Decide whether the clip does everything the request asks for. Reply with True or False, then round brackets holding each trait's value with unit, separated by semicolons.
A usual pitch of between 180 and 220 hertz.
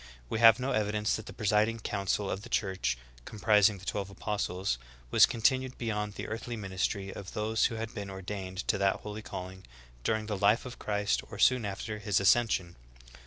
False (105 Hz)